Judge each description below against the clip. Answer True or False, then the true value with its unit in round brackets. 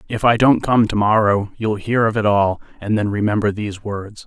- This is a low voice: True (105 Hz)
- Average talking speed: False (225 wpm)